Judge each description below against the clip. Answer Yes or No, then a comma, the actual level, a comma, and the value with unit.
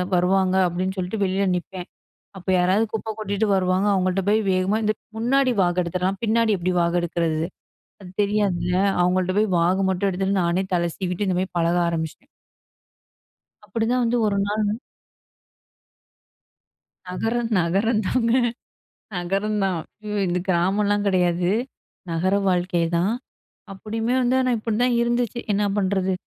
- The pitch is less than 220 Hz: Yes, high, 190 Hz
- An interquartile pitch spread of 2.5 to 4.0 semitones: Yes, average, 3.1 semitones